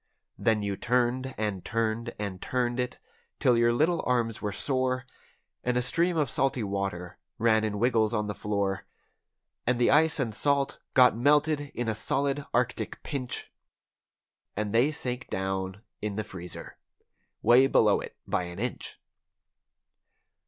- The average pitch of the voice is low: Yes, low, 120 Hz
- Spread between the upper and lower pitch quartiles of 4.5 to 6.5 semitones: No, average, 3.7 semitones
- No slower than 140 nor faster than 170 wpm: Yes, average, 145 wpm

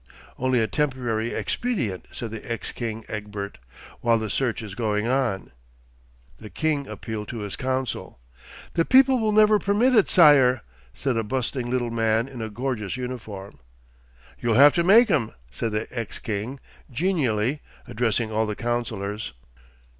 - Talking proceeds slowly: No, average, 155 wpm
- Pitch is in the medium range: No, low, 120 Hz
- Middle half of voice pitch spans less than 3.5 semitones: No, average, 4.0 semitones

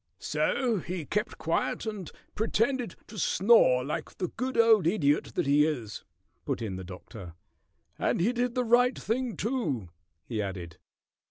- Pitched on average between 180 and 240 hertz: Yes, medium, 185 Hz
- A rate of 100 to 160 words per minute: Yes, average, 155 wpm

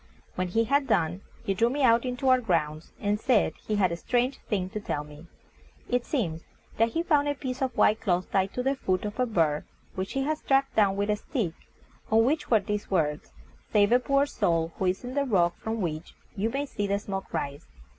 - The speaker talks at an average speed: No, fast, 225 wpm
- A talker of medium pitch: No, high, 210 Hz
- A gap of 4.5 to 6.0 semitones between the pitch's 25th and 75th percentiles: Yes, wide, 5.6 semitones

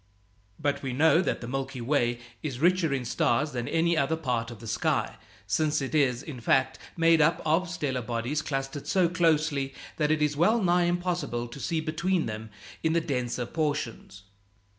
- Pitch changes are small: No, average, 4.5 semitones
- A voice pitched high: No, medium, 145 Hz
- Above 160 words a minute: Yes, average, 180 wpm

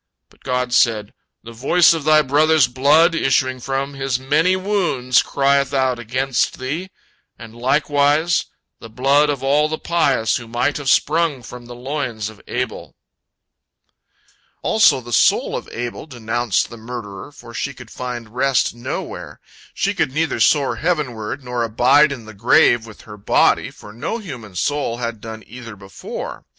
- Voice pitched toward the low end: Yes, low, 130 Hz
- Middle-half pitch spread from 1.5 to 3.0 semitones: No, average, 3.8 semitones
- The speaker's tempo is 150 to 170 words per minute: Yes, average, 160 wpm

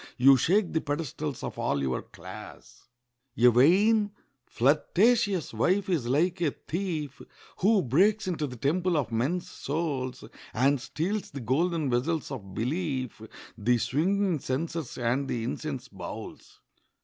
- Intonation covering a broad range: Yes, wide, 5.9 semitones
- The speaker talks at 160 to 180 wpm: No, slow, 135 wpm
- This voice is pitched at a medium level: Yes, medium, 150 Hz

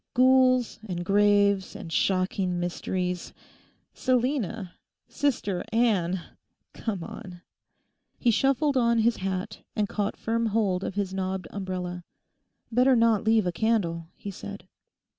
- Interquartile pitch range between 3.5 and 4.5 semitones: Yes, average, 3.9 semitones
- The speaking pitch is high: Yes, high, 205 Hz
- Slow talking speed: Yes, slow, 120 wpm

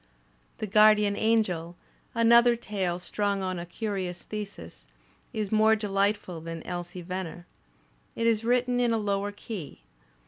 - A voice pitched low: No, high, 205 Hz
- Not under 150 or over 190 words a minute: No, slow, 135 wpm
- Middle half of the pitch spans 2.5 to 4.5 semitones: Yes, average, 3.6 semitones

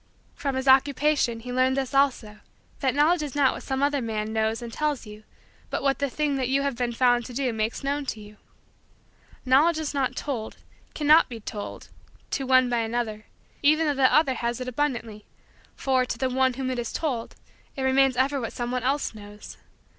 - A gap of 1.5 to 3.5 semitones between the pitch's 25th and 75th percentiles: Yes, average, 3.0 semitones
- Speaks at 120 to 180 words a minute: No, average, 200 wpm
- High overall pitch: Yes, very high, 260 Hz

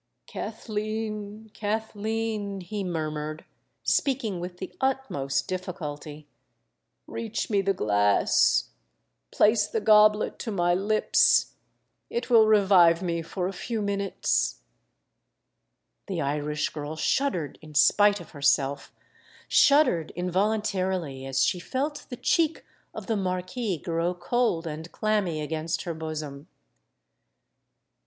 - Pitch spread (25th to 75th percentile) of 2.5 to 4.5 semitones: No, average, 5.2 semitones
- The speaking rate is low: Yes, slow, 105 wpm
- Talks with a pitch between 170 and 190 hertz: Yes, medium, 185 Hz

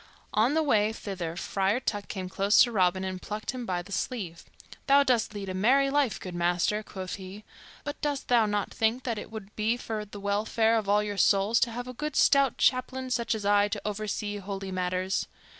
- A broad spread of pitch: No, average, 3.7 semitones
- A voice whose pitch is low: No, high, 210 Hz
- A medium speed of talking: No, fast, 210 wpm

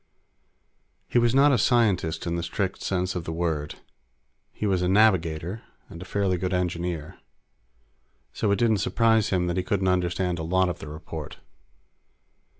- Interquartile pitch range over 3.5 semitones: No, average, 3.0 semitones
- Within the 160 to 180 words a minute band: Yes, average, 170 wpm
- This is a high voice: No, very low, 90 Hz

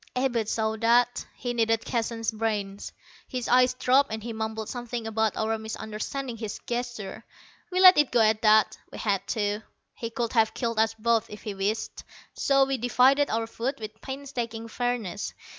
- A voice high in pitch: Yes, high, 225 Hz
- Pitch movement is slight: Yes, narrow, 2.1 semitones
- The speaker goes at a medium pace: Yes, average, 175 wpm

